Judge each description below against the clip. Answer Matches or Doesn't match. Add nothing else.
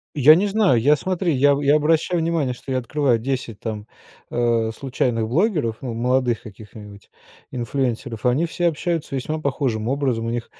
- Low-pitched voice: Matches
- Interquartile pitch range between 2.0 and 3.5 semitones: Doesn't match